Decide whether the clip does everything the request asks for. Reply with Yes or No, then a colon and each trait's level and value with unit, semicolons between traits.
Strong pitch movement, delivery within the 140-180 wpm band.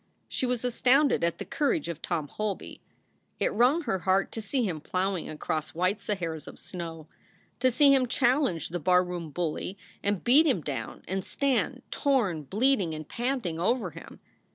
Yes: wide, 6.8 semitones; average, 170 wpm